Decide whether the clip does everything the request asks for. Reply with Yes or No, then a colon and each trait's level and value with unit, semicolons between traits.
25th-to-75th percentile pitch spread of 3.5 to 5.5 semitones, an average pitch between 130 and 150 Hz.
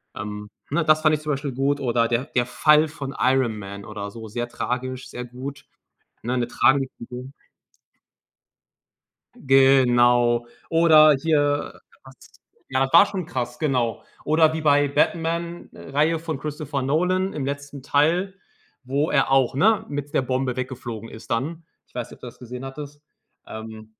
Yes: average, 3.8 semitones; low, 135 Hz